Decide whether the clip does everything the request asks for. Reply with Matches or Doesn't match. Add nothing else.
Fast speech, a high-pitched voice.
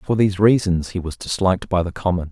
Doesn't match